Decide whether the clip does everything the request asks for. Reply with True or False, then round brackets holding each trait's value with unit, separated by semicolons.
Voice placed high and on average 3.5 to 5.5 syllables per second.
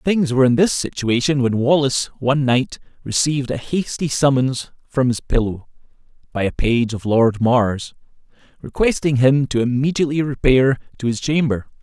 False (130 Hz; 5.0 syllables/s)